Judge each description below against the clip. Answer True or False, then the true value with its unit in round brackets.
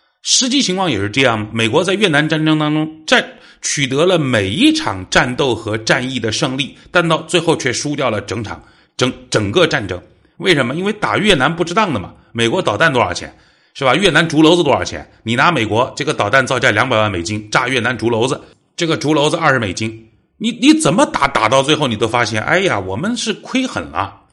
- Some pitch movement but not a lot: False (8.0 semitones)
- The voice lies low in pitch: False (145 Hz)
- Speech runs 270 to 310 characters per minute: False (320 characters per minute)